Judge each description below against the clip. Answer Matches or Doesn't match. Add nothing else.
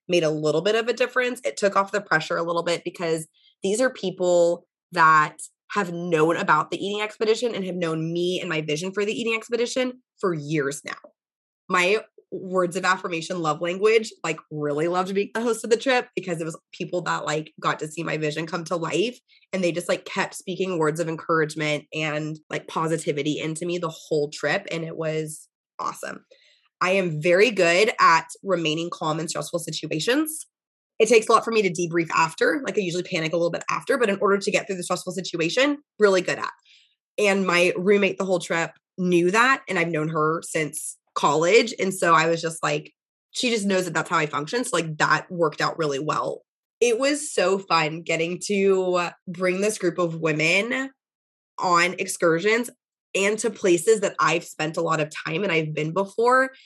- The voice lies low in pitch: Doesn't match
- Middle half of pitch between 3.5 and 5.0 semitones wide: Matches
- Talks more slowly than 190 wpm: Doesn't match